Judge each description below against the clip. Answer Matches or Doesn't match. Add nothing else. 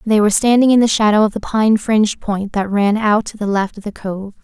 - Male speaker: Doesn't match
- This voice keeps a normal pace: Doesn't match